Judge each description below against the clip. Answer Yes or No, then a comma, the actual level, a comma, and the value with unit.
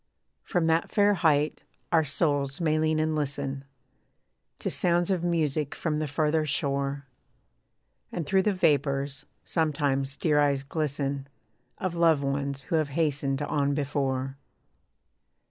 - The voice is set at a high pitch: No, medium, 145 Hz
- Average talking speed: No, slow, 130 wpm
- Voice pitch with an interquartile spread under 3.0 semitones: Yes, narrow, 2.5 semitones